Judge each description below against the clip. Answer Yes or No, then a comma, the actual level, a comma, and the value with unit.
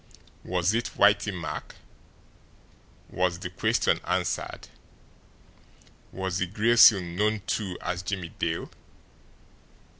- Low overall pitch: Yes, very low, 90 Hz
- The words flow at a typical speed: No, slow, 100 wpm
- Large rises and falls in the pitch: No, average, 3.0 semitones